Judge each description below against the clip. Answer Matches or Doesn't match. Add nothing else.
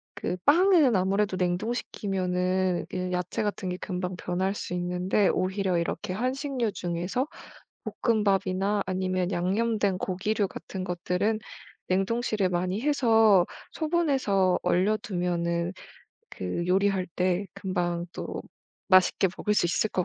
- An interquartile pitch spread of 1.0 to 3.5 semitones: Matches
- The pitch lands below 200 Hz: Matches